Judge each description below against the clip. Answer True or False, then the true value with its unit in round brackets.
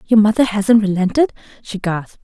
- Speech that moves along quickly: False (160 wpm)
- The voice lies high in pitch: True (210 Hz)